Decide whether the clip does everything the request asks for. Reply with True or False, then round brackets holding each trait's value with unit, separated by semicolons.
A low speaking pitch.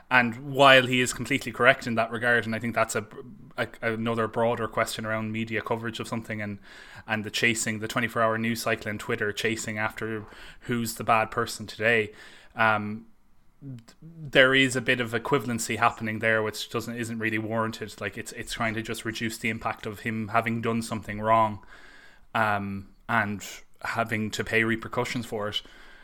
True (115 Hz)